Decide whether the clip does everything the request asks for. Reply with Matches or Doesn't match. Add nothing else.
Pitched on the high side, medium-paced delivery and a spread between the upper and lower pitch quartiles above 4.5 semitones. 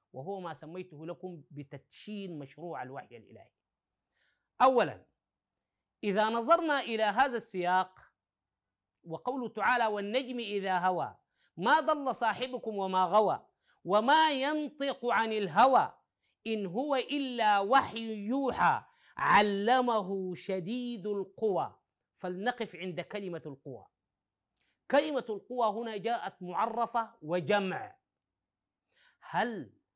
Matches